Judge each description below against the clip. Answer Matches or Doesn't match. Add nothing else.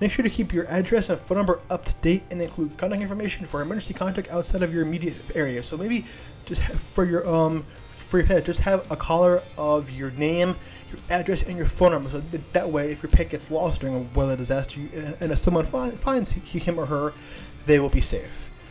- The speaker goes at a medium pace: Doesn't match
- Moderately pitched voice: Matches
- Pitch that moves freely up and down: Doesn't match